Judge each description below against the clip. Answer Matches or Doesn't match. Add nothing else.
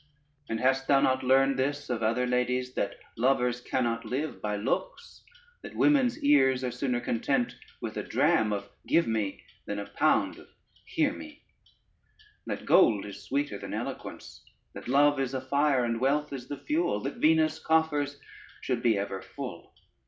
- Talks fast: Doesn't match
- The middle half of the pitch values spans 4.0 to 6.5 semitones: Doesn't match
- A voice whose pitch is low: Matches